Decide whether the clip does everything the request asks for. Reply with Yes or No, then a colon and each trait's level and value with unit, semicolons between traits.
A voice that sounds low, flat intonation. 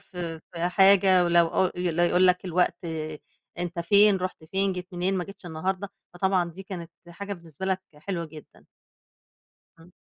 No: medium, 180 Hz; narrow, 1.9 semitones